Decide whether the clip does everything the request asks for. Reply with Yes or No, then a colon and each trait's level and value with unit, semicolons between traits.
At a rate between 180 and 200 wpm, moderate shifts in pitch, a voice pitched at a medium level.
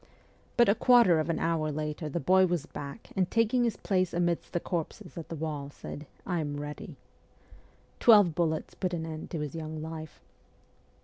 Yes: average, 190 wpm; average, 3.1 semitones; medium, 165 Hz